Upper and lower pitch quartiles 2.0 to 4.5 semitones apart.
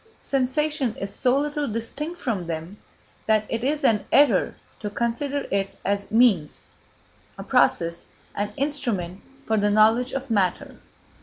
No: wide, 5.4 semitones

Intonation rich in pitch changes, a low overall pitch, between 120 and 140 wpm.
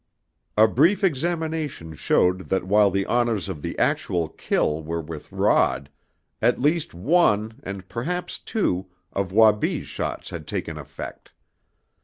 Yes: wide, 8.9 semitones; low, 105 Hz; slow, 135 wpm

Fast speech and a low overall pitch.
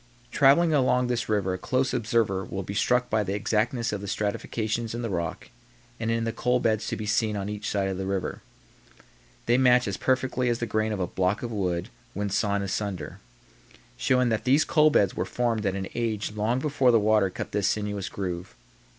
Yes: fast, 210 wpm; low, 110 Hz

